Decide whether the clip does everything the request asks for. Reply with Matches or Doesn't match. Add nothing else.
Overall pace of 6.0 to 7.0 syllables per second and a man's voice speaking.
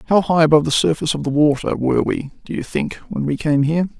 Matches